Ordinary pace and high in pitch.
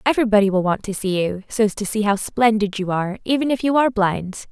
No: fast, 240 wpm; high, 210 Hz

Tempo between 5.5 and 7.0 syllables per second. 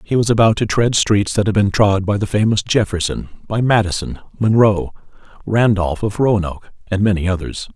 No: 5.3 syllables/s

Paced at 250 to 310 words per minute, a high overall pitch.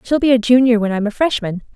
Yes: fast, 275 wpm; high, 235 Hz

